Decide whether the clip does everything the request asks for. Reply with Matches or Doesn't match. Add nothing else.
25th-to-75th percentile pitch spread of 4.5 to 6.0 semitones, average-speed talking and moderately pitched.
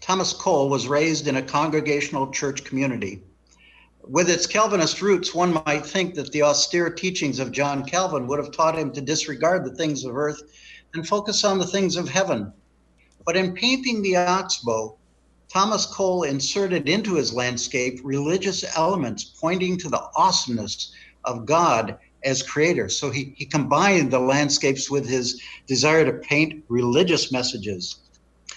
Matches